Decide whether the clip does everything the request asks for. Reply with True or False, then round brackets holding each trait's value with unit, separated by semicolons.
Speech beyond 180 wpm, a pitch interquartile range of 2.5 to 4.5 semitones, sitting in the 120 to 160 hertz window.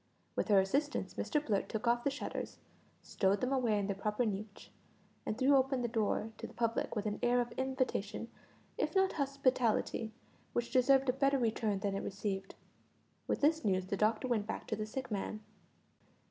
False (190 wpm; 4.1 semitones; 230 Hz)